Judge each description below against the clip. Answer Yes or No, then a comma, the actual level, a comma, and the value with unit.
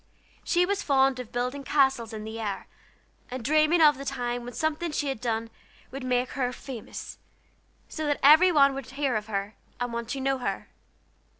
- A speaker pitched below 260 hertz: No, very high, 265 Hz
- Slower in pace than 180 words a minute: No, average, 185 wpm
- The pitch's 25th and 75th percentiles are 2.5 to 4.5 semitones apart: Yes, average, 3.3 semitones